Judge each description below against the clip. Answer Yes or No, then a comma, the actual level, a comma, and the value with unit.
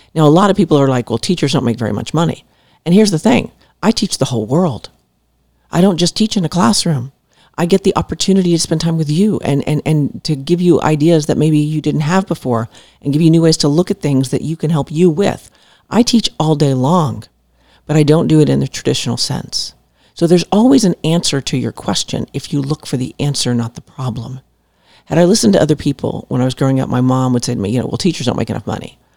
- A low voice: No, medium, 150 Hz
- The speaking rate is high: Yes, fast, 255 wpm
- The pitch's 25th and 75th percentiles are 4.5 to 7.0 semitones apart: Yes, average, 5.1 semitones